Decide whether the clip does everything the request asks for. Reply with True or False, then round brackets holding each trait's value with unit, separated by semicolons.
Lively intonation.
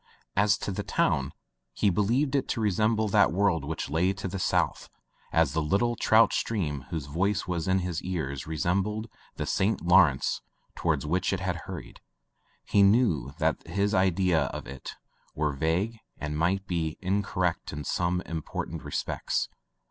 False (3.9 semitones)